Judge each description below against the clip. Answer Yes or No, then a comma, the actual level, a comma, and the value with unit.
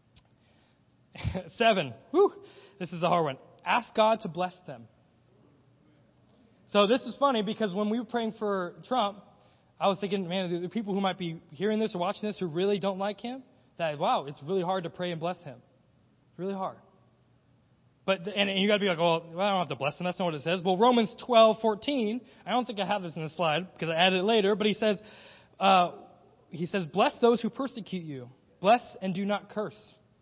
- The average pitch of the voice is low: No, high, 190 Hz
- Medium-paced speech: No, fast, 215 wpm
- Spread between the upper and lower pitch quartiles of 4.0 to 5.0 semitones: Yes, average, 4.3 semitones